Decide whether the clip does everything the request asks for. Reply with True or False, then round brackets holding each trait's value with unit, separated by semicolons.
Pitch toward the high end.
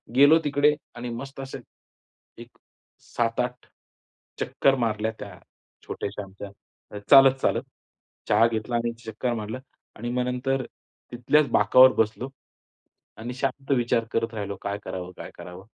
False (120 Hz)